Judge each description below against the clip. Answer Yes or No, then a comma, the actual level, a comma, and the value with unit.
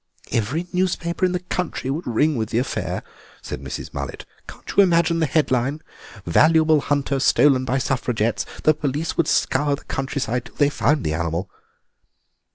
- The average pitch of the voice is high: No, medium, 140 Hz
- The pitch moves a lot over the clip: No, average, 4.4 semitones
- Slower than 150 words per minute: No, average, 165 wpm